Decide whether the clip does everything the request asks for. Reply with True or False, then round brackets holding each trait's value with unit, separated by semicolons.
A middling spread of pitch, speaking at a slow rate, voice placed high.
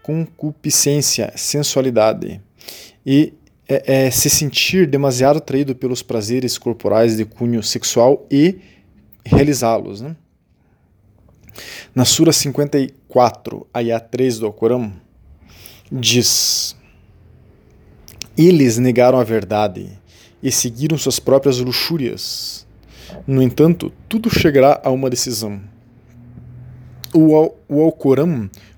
False (4.2 semitones; 90 wpm; 125 Hz)